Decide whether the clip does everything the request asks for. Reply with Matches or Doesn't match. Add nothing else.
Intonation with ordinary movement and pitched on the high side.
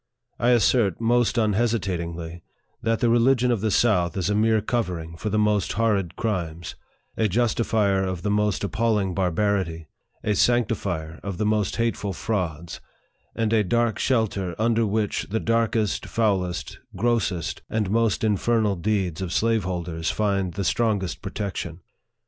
Doesn't match